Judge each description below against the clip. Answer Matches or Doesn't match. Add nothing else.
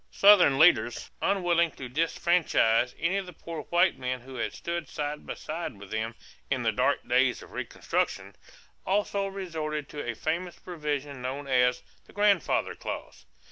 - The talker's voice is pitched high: Doesn't match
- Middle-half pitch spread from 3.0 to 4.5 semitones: Doesn't match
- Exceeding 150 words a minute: Matches